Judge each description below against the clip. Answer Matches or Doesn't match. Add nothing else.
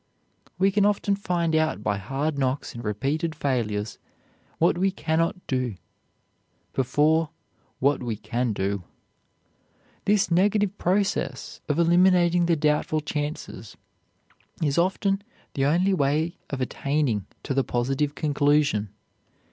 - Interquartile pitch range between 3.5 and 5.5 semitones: Matches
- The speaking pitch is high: Doesn't match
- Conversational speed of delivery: Doesn't match